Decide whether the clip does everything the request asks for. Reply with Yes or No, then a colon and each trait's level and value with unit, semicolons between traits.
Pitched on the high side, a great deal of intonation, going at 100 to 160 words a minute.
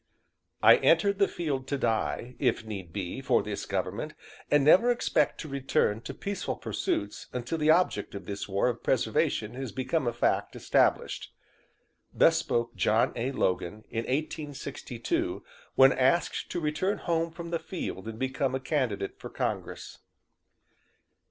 No: low, 130 Hz; wide, 5.8 semitones; average, 150 wpm